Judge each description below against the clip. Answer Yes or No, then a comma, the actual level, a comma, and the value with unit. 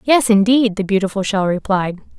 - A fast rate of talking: No, average, 165 wpm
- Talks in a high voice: Yes, high, 205 Hz